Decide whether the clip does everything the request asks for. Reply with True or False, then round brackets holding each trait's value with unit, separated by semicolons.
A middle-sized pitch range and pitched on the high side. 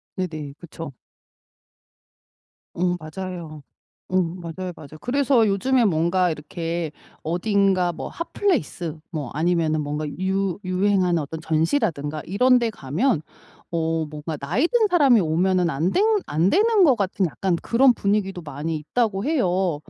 False (4.5 semitones; 180 Hz)